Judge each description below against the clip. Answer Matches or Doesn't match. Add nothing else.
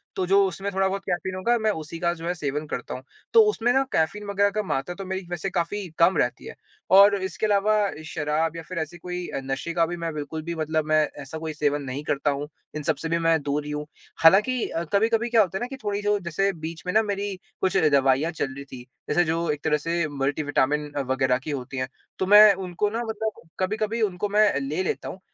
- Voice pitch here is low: Doesn't match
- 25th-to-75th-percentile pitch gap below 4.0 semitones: Doesn't match